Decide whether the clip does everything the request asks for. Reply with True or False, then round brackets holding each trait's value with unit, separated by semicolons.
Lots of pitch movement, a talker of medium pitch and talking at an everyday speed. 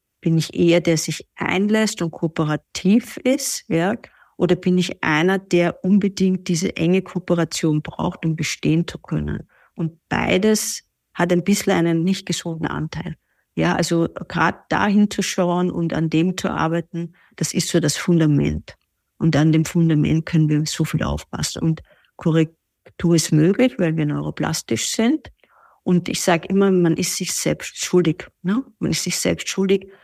False (2.8 semitones; 175 Hz; 160 wpm)